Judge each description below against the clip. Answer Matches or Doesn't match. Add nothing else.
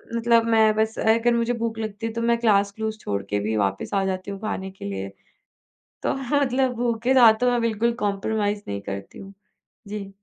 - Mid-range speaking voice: Doesn't match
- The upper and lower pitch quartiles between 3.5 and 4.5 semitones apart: Doesn't match